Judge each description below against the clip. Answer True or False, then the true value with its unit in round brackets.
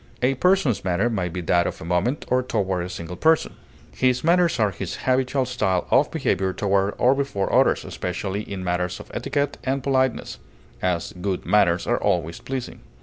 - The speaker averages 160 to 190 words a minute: True (180 wpm)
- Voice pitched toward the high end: False (100 Hz)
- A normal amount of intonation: False (6.3 semitones)